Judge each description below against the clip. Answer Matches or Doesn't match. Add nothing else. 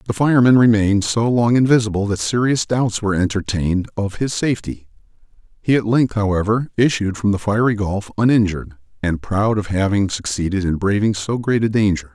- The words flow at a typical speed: Matches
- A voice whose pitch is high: Doesn't match